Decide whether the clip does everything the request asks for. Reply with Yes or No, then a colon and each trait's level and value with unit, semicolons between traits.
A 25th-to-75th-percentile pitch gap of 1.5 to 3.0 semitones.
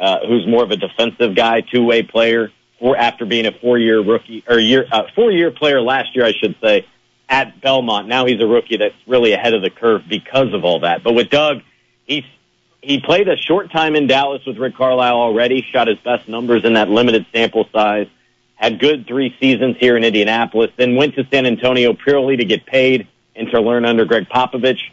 Yes: narrow, 2.6 semitones